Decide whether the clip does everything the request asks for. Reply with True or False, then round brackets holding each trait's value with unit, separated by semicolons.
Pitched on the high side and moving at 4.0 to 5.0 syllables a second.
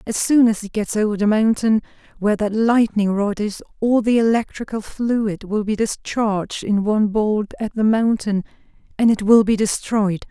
True (215 Hz; 4.8 syllables/s)